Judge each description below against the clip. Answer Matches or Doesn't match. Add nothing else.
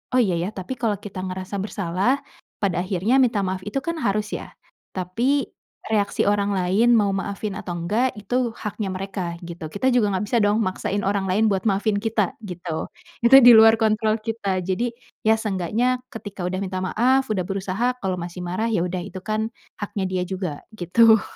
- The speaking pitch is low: Doesn't match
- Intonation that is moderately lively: Matches